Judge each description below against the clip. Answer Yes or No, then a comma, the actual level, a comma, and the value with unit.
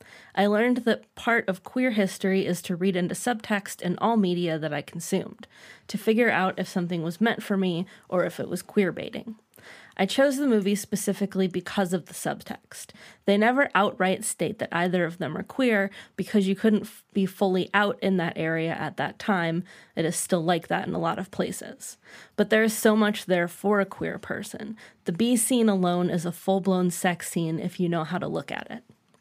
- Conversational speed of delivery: No, fast, 210 wpm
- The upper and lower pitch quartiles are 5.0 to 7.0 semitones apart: No, average, 3.2 semitones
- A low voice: No, high, 195 Hz